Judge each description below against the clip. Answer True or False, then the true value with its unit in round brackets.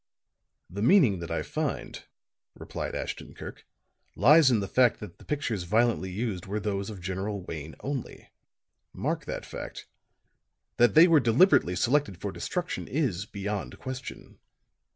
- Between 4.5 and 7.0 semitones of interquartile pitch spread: True (5.5 semitones)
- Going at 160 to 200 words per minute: False (145 wpm)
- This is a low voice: True (105 Hz)